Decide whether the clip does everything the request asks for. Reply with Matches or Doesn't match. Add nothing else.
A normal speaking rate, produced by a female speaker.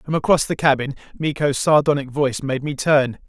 Doesn't match